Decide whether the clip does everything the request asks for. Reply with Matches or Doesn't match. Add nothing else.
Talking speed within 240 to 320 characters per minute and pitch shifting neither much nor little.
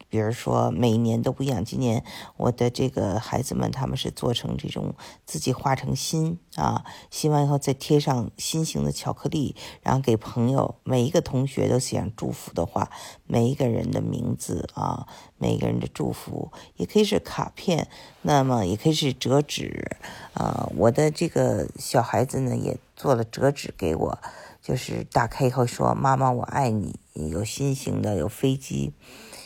Matches